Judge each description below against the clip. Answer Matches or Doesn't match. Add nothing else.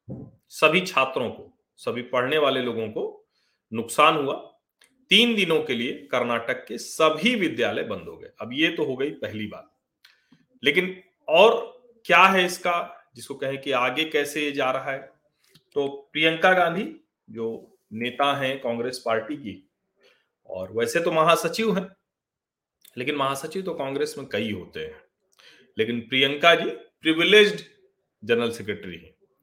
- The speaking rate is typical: Matches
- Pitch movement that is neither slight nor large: Doesn't match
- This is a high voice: Doesn't match